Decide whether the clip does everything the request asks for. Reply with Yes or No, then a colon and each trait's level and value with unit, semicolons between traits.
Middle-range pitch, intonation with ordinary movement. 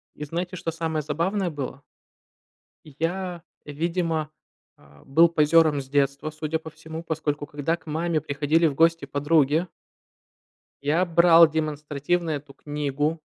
No: medium, 155 Hz; narrow, 2.2 semitones